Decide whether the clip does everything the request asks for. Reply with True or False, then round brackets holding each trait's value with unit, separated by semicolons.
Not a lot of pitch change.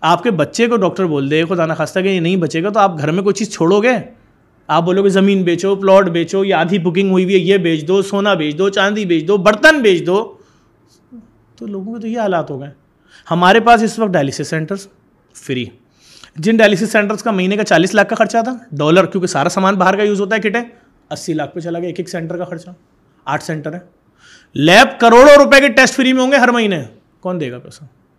False (4.5 semitones)